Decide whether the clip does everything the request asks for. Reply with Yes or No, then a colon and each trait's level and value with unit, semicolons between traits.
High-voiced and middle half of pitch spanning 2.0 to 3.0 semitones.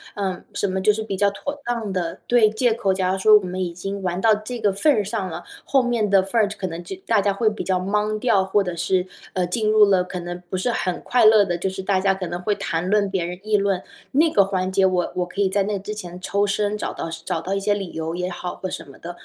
Yes: high, 195 Hz; narrow, 2.6 semitones